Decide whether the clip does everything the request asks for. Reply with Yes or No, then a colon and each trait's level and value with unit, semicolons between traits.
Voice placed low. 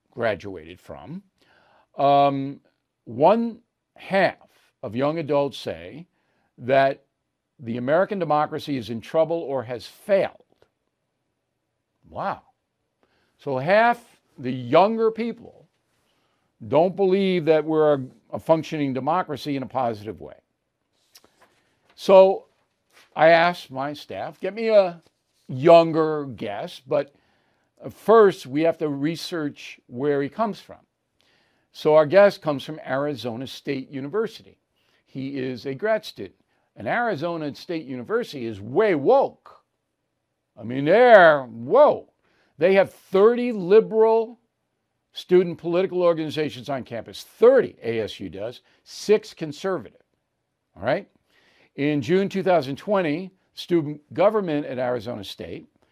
No: medium, 155 Hz